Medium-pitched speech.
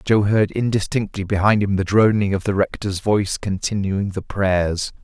No: low, 100 Hz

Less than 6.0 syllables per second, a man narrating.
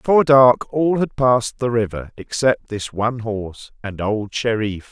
Yes: 4.6 syllables/s; male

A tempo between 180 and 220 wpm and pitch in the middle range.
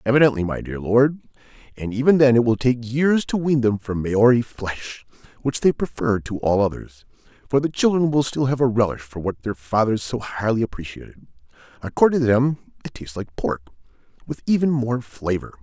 No: average, 190 wpm; low, 120 Hz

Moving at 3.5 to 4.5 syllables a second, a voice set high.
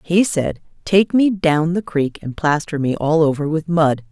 No: 4.3 syllables/s; medium, 160 Hz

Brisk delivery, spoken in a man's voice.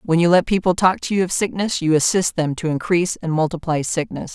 No: fast, 235 wpm; female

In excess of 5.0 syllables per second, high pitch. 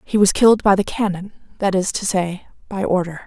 Yes: 5.7 syllables/s; high, 195 Hz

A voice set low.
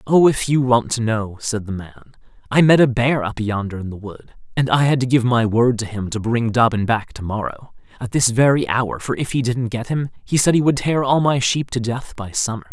Yes: low, 120 Hz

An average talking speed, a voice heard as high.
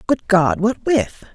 Yes: average, 180 wpm; high, 230 Hz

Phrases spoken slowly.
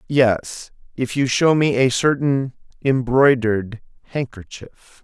Yes: slow, 105 wpm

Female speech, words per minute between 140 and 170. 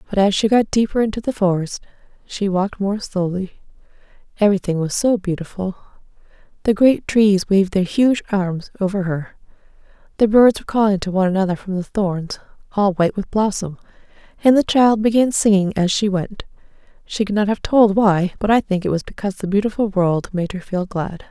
No: female; average, 185 wpm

